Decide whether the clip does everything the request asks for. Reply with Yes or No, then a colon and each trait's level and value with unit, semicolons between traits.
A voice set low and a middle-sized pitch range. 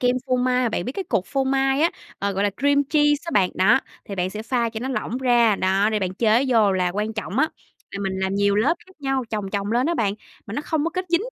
No: high, 235 Hz; average, 5.0 semitones